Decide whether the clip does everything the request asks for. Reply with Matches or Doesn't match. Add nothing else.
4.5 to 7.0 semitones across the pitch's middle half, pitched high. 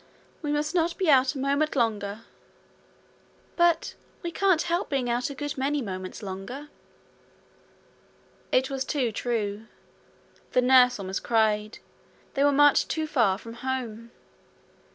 Matches